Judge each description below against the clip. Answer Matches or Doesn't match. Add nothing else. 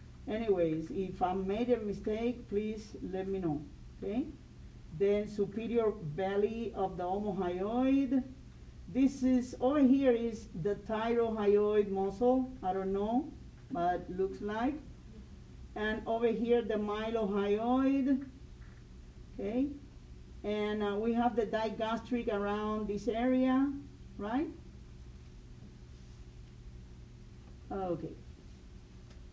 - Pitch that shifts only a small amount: Doesn't match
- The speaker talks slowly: Matches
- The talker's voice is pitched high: Matches